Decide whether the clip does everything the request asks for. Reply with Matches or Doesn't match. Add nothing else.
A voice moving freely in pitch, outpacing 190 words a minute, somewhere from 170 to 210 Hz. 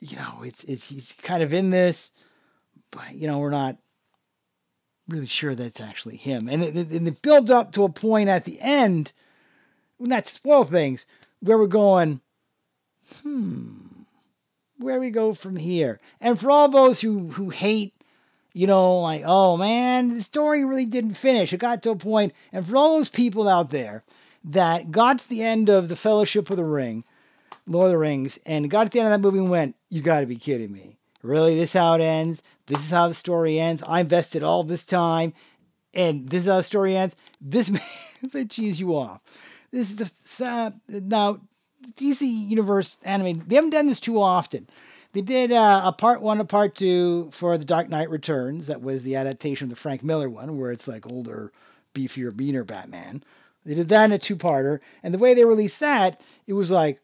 Matches